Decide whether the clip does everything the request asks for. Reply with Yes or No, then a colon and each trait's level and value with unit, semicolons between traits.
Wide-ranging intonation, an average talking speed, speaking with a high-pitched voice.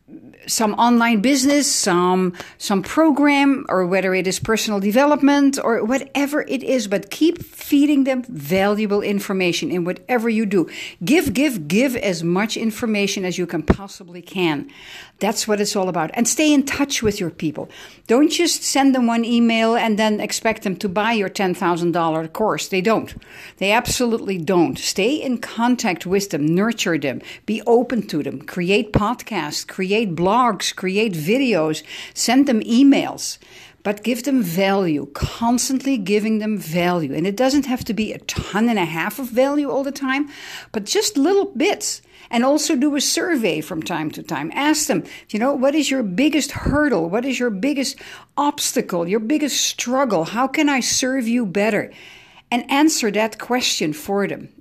Yes: wide, 5.9 semitones; average, 175 wpm; high, 225 Hz